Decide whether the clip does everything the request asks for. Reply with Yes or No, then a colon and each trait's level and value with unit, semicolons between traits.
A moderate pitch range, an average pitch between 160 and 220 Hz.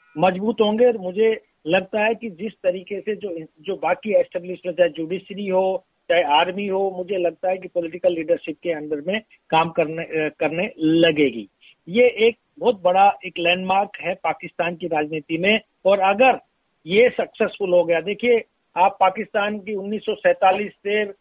Yes: average, 3.5 semitones; medium, 185 Hz